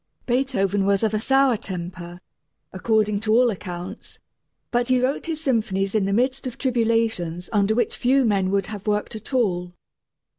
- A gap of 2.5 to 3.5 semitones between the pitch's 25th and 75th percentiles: No, average, 4.1 semitones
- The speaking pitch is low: No, high, 215 Hz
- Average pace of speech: Yes, average, 170 wpm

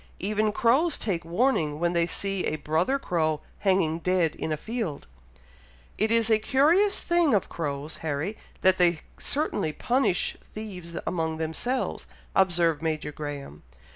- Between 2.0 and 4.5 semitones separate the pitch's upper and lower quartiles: No, wide, 5.6 semitones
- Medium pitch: Yes, medium, 180 Hz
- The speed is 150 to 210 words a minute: No, average, 140 wpm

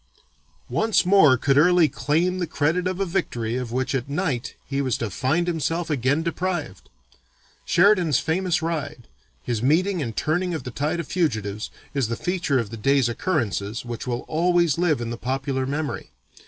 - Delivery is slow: No, average, 175 wpm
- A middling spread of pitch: No, wide, 5.7 semitones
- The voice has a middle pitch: Yes, medium, 145 Hz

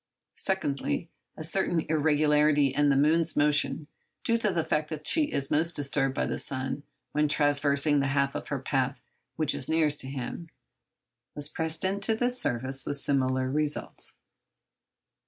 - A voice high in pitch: No, medium, 150 Hz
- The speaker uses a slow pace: No, average, 155 wpm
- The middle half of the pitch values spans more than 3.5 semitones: No, narrow, 2.4 semitones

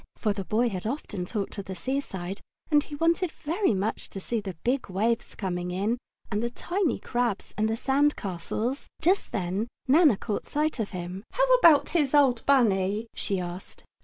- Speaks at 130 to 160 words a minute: No, average, 185 wpm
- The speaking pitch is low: No, high, 225 Hz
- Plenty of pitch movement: Yes, wide, 6.7 semitones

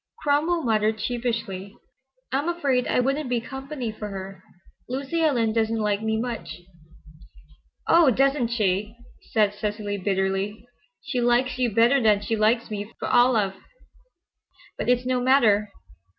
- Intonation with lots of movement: No, average, 3.7 semitones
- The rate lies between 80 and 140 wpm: Yes, slow, 135 wpm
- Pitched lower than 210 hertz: No, high, 230 Hz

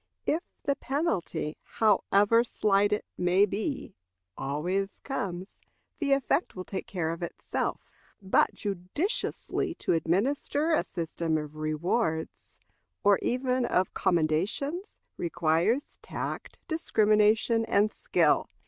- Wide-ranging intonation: Yes, wide, 6.6 semitones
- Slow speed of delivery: Yes, slow, 110 wpm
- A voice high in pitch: Yes, high, 200 Hz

